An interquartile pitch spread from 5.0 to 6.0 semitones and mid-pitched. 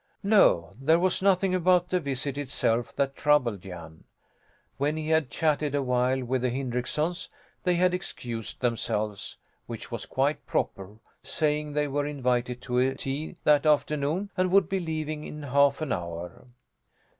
No: average, 4.2 semitones; medium, 145 Hz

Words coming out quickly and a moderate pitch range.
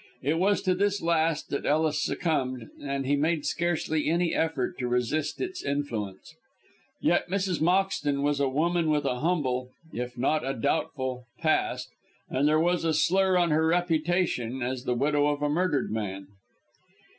No: average, 165 wpm; average, 4.4 semitones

